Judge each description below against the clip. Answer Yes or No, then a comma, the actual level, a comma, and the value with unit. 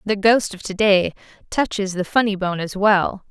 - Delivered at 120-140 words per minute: No, average, 200 wpm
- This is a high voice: Yes, high, 200 Hz